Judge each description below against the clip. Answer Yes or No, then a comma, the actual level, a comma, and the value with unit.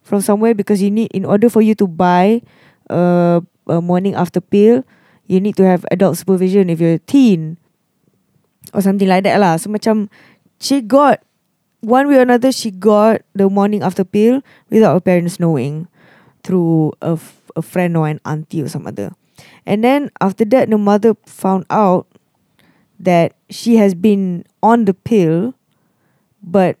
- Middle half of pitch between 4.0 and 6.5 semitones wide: No, average, 3.5 semitones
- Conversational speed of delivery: Yes, average, 170 wpm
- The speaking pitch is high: Yes, high, 195 Hz